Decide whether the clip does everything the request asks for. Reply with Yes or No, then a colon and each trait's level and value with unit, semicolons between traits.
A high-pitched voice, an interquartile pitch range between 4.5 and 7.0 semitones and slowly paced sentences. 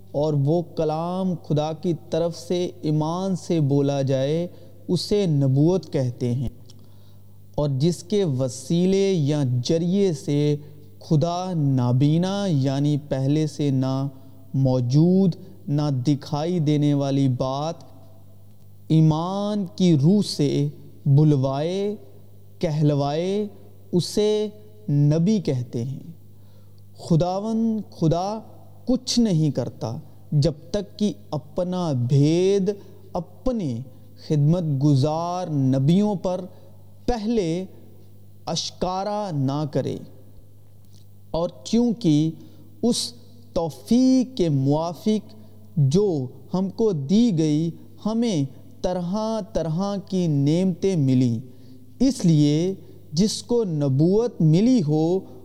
No: medium, 155 Hz; wide, 5.6 semitones; slow, 95 wpm